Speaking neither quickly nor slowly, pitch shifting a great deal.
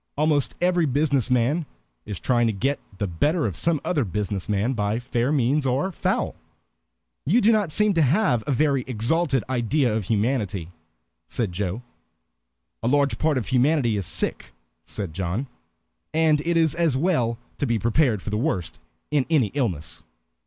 Yes: average, 165 wpm; wide, 6.1 semitones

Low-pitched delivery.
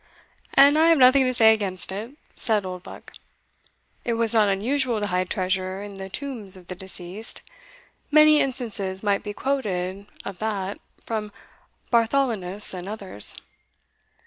No: high, 210 Hz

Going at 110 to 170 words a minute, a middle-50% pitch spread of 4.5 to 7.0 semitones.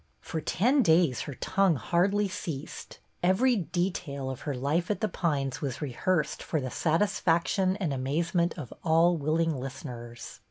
Yes: average, 155 wpm; average, 5.0 semitones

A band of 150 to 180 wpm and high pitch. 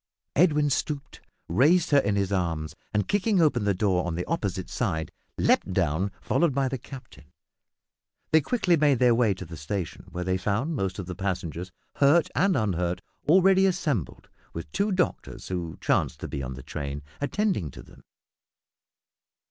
No: average, 170 wpm; low, 105 Hz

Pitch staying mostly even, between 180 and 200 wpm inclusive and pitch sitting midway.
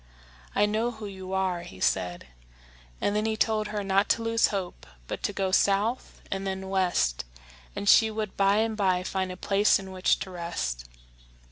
No: narrow, 2.3 semitones; average, 190 wpm; high, 195 Hz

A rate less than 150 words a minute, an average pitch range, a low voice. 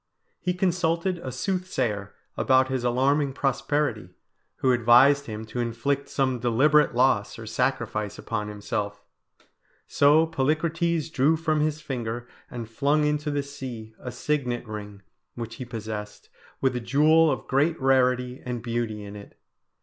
Yes: average, 140 wpm; average, 4.5 semitones; low, 130 Hz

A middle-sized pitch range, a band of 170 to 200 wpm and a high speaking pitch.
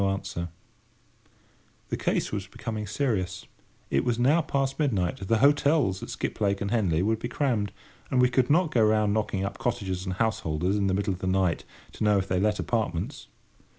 No: average, 4.2 semitones; average, 190 wpm; low, 105 Hz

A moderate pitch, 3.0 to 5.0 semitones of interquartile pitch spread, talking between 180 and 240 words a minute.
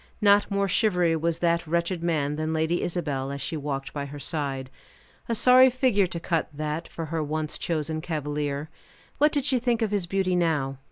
Yes: medium, 165 Hz; average, 4.6 semitones; average, 190 wpm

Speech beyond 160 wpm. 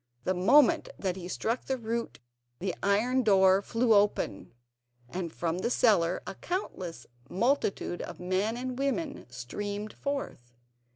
No: slow, 135 wpm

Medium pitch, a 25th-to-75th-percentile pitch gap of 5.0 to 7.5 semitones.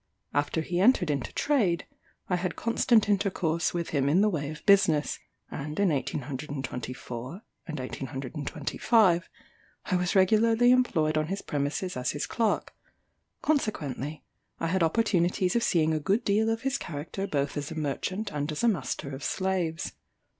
Yes: medium, 170 Hz; wide, 5.4 semitones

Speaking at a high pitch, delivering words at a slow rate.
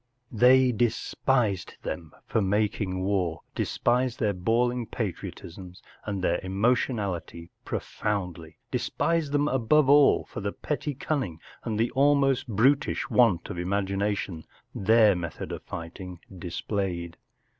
No: low, 105 Hz; slow, 115 wpm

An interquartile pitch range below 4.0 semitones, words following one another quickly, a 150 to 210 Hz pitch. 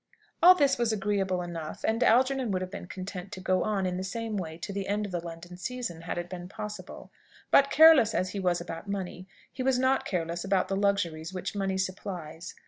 Yes: average, 3.3 semitones; fast, 220 wpm; high, 190 Hz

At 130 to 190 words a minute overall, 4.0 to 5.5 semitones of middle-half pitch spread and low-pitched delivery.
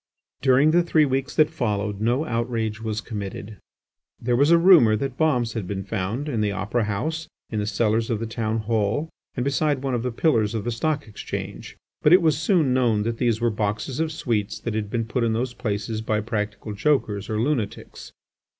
No: fast, 205 wpm; average, 4.4 semitones; low, 115 Hz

